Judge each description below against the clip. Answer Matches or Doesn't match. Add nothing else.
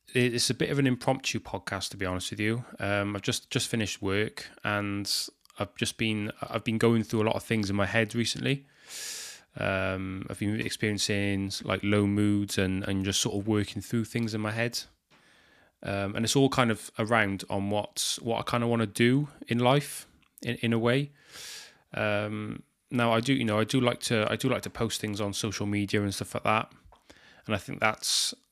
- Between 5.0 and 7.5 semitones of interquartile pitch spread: Doesn't match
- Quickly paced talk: Matches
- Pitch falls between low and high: Doesn't match